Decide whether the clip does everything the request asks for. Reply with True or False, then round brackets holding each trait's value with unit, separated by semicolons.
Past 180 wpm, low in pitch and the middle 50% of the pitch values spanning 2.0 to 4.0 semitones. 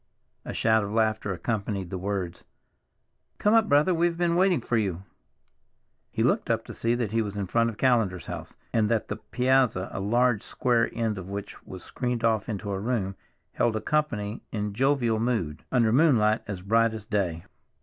True (190 wpm; 110 Hz; 3.5 semitones)